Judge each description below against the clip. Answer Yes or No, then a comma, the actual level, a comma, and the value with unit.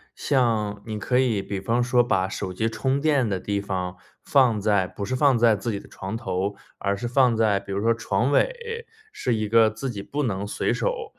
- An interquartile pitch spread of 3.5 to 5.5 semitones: Yes, average, 4.1 semitones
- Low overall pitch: Yes, low, 110 Hz